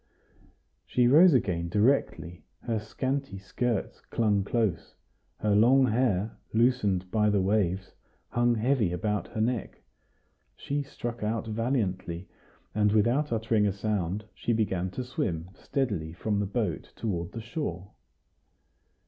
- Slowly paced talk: Yes, slow, 130 wpm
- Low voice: Yes, low, 110 Hz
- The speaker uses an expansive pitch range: No, average, 4.0 semitones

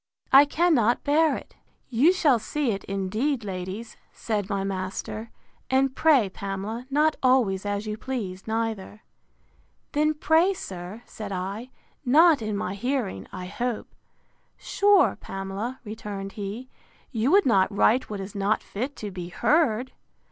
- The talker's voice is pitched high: Yes, high, 220 Hz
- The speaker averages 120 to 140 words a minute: Yes, slow, 135 wpm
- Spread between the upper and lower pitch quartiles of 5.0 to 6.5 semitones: Yes, wide, 5.4 semitones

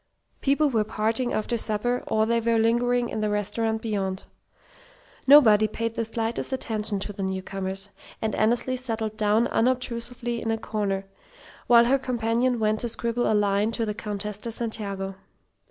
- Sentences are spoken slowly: No, average, 160 wpm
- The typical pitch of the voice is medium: No, high, 225 Hz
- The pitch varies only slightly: Yes, narrow, 2.2 semitones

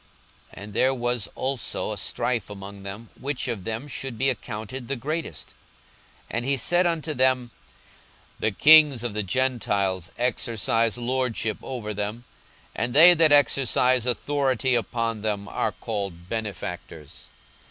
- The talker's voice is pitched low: Yes, low, 120 Hz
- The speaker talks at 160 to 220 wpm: No, average, 140 wpm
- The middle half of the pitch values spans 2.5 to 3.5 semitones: No, average, 3.9 semitones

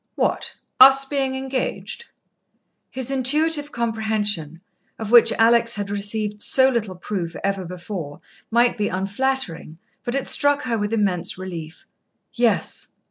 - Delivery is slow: Yes, slow, 130 wpm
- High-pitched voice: Yes, high, 220 Hz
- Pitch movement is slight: No, average, 5.2 semitones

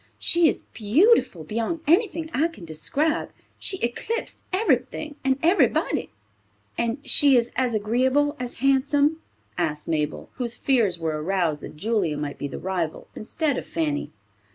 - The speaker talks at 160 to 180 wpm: No, average, 145 wpm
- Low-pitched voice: No, high, 240 Hz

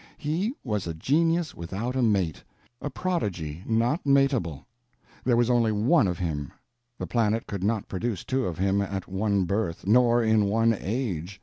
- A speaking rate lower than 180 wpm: Yes, average, 170 wpm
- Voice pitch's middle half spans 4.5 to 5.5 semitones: Yes, average, 4.8 semitones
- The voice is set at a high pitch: No, low, 110 Hz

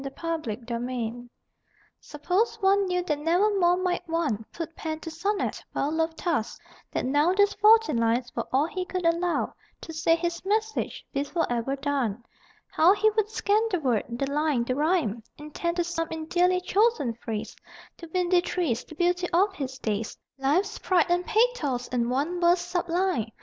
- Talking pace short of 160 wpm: No, average, 175 wpm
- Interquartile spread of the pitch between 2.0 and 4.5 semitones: No, average, 5.2 semitones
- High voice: Yes, very high, 330 Hz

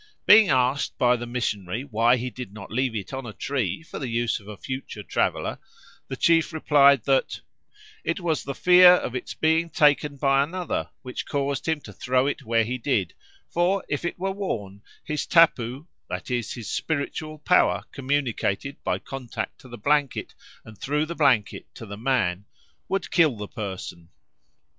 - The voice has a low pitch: Yes, low, 130 Hz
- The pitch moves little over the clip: No, average, 4.7 semitones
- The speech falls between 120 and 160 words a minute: No, average, 175 wpm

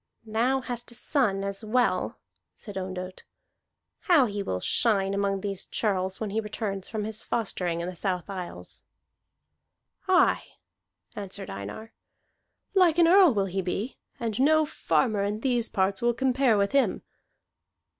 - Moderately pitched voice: No, high, 210 Hz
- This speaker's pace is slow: No, average, 145 wpm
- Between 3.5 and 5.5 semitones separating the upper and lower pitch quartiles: Yes, average, 4.0 semitones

